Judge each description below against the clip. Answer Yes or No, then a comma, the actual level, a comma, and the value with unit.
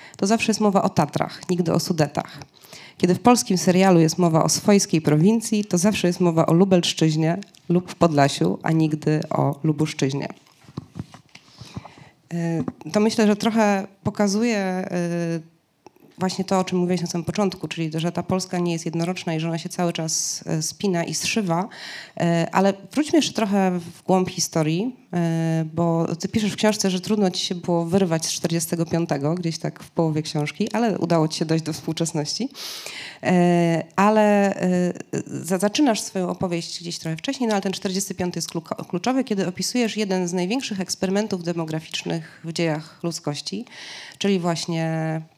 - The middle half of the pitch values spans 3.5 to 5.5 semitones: No, average, 3.0 semitones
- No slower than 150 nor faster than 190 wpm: Yes, average, 155 wpm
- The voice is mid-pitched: Yes, medium, 175 Hz